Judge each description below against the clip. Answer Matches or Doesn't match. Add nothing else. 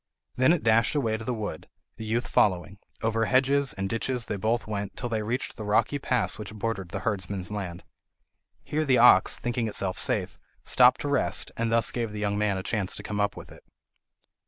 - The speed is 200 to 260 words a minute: Matches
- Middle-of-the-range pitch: Doesn't match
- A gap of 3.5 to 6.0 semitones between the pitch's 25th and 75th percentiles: Doesn't match